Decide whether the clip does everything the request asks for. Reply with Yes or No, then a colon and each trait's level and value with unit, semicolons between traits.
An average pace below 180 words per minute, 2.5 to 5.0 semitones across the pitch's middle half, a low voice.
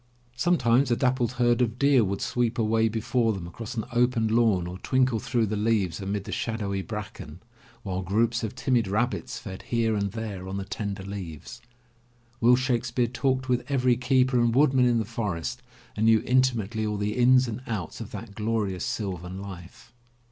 No: average, 185 wpm; average, 3.6 semitones; low, 115 Hz